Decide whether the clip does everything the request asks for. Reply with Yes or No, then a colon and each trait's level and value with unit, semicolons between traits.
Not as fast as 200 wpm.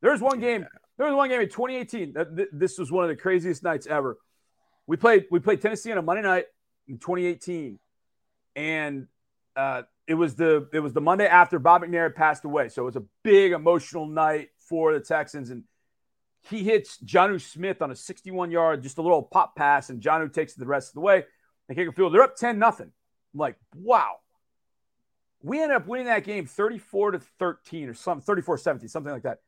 No: fast, 205 wpm